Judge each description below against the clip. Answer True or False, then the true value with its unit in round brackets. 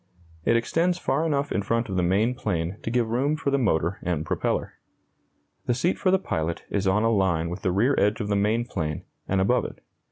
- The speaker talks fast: True (225 wpm)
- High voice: False (105 Hz)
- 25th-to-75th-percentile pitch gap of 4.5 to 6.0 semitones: True (5.1 semitones)